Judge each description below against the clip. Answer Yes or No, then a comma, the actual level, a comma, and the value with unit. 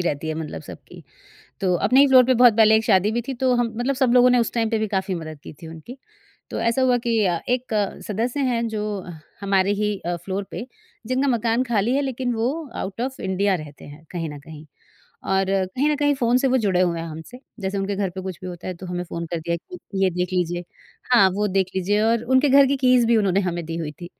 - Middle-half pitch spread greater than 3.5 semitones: Yes, wide, 5.5 semitones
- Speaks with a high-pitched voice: Yes, high, 210 Hz